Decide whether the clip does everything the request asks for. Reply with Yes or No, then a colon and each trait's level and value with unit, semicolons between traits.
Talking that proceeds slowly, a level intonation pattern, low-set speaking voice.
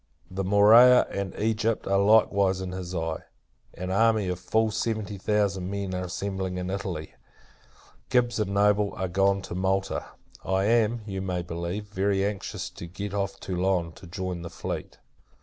No: average, 165 wpm; narrow, 2.1 semitones; very low, 95 Hz